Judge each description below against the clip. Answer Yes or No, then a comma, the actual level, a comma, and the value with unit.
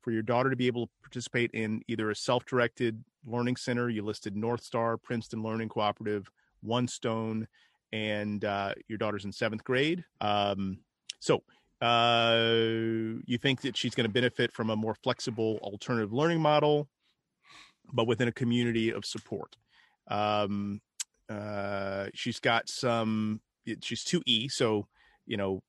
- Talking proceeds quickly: No, average, 150 wpm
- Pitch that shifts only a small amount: Yes, narrow, 2.2 semitones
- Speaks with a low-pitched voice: Yes, low, 115 Hz